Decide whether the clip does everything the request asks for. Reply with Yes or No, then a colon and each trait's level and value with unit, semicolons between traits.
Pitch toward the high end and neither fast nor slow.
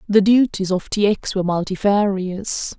Yes: high, 200 Hz; average, 150 wpm